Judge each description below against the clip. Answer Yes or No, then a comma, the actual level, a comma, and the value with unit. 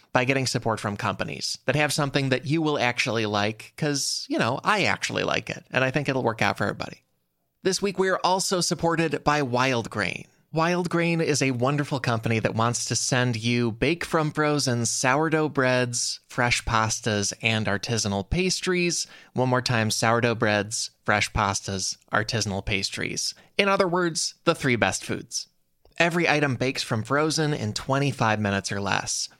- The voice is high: No, low, 125 Hz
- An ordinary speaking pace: Yes, average, 170 wpm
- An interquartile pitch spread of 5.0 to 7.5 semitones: Yes, wide, 5.5 semitones